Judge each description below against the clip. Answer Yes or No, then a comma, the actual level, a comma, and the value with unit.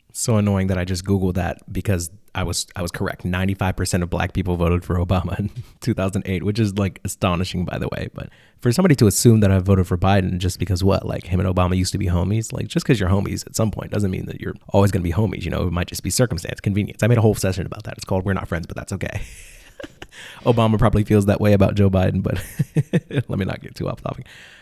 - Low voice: Yes, low, 100 Hz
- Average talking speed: No, fast, 265 wpm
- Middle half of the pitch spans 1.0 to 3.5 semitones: Yes, average, 2.9 semitones